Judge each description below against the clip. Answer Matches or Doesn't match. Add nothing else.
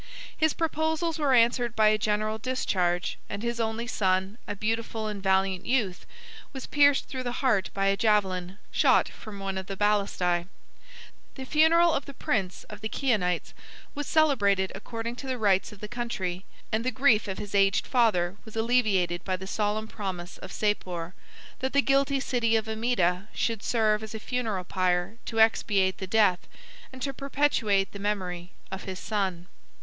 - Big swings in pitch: Doesn't match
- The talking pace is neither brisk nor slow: Matches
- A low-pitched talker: Doesn't match